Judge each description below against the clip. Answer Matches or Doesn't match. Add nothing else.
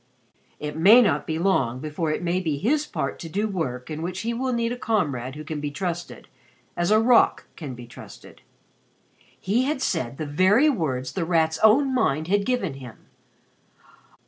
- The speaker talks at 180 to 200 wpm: Matches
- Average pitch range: Doesn't match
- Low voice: Doesn't match